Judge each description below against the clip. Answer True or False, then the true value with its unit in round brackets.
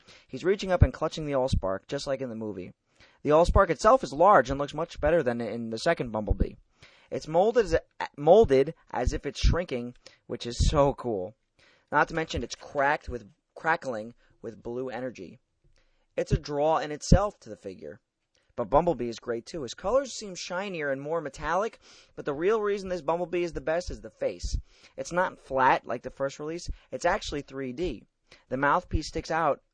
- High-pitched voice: False (140 Hz)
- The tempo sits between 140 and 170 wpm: False (185 wpm)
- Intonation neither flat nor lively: False (6.2 semitones)